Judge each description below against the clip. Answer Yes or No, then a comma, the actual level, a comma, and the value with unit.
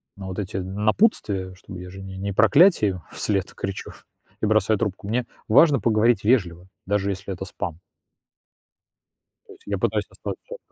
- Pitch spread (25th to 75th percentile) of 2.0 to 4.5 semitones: Yes, narrow, 2.6 semitones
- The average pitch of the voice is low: Yes, low, 100 Hz